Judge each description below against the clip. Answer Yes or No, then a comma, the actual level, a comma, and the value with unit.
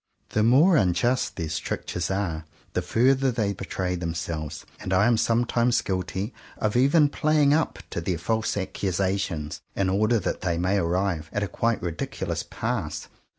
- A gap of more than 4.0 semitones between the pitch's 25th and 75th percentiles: Yes, average, 5.1 semitones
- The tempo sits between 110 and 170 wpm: Yes, average, 155 wpm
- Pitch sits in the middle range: No, low, 100 Hz